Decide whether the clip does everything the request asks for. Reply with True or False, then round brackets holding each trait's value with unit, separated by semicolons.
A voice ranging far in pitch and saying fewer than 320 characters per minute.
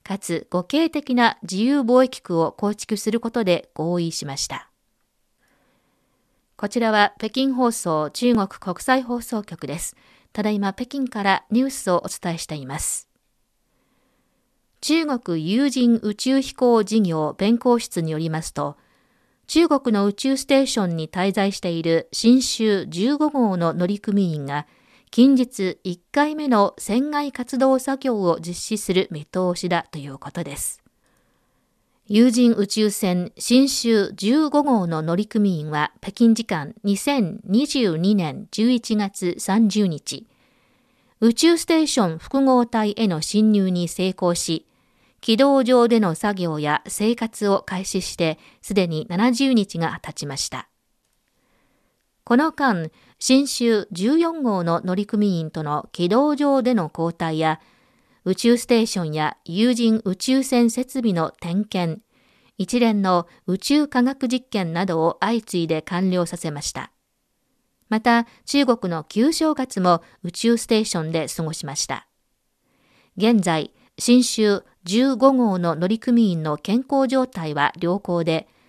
True (6.0 semitones; 230 characters per minute)